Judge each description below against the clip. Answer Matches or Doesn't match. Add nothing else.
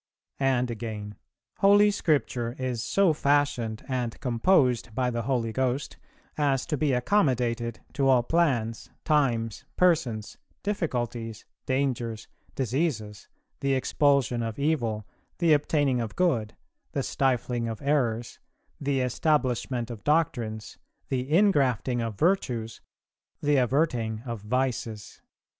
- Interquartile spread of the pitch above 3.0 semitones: Matches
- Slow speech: Matches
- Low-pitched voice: Matches